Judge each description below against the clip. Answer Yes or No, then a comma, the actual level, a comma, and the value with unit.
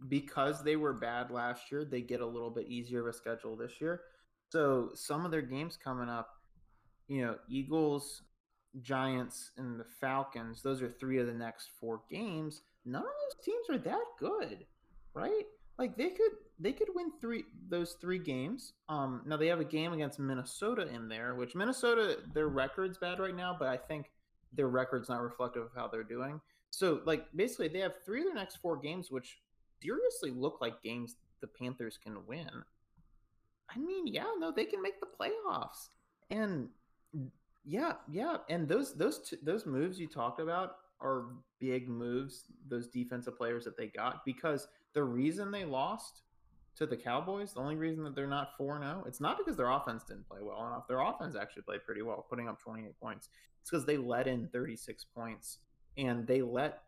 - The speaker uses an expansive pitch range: Yes, wide, 6.3 semitones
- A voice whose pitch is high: No, low, 135 Hz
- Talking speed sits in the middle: Yes, average, 190 wpm